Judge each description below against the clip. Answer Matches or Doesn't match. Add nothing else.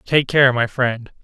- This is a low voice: Matches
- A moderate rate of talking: Matches